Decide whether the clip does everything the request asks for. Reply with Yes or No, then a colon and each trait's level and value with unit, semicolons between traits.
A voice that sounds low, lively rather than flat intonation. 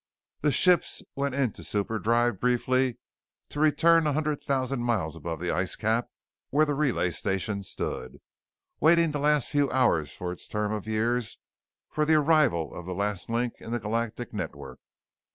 Yes: low, 120 Hz; wide, 6.2 semitones